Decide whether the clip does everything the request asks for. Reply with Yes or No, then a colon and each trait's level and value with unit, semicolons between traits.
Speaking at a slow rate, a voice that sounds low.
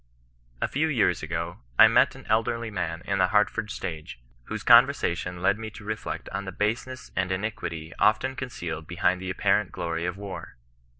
No: average, 180 wpm; very low, 95 Hz